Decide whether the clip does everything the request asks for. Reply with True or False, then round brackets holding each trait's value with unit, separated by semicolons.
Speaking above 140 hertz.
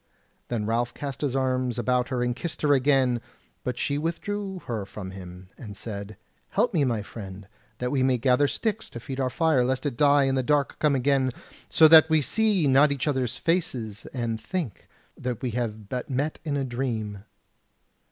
False (130 Hz)